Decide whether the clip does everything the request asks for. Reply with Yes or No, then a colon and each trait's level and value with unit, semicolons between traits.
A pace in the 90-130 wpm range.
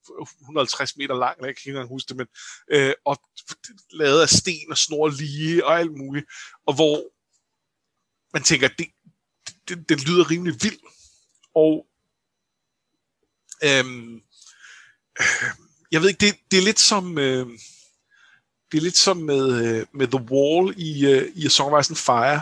No: average, 160 wpm